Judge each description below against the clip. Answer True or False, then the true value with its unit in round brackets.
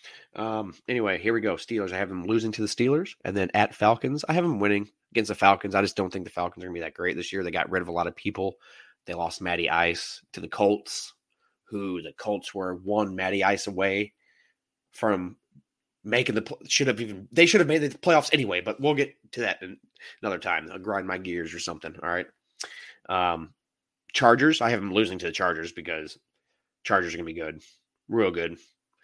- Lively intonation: False (3.6 semitones)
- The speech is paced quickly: True (220 wpm)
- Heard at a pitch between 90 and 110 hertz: True (100 Hz)